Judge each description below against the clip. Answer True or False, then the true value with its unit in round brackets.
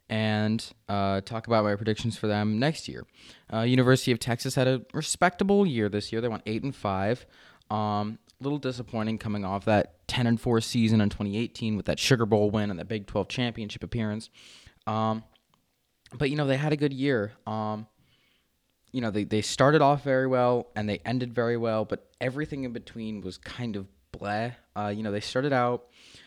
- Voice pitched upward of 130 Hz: False (110 Hz)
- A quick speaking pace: False (195 wpm)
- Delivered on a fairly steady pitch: False (3.0 semitones)